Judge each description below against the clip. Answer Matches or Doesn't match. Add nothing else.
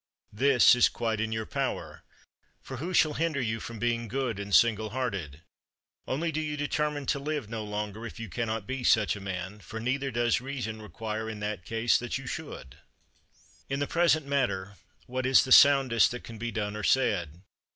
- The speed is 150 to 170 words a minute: Doesn't match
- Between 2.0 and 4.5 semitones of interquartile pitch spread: Matches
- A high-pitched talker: Doesn't match